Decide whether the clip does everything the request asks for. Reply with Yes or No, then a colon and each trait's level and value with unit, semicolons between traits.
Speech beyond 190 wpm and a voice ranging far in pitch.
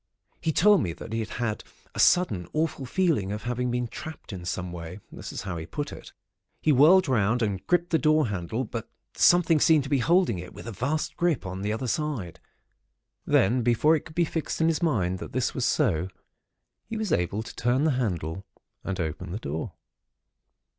Yes: average, 200 wpm; wide, 8.3 semitones